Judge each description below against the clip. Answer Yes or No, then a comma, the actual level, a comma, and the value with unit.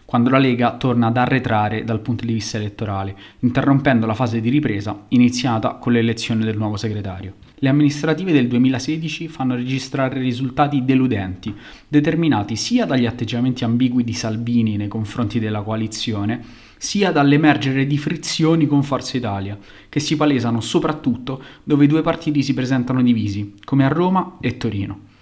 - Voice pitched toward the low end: Yes, low, 125 Hz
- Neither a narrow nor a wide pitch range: Yes, average, 4.1 semitones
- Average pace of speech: Yes, average, 150 wpm